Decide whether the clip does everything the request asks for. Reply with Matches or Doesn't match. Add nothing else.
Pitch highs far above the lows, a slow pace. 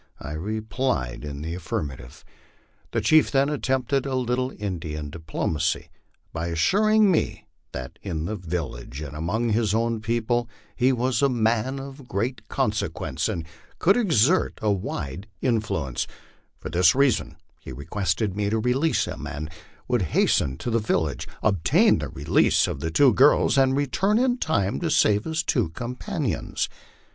Doesn't match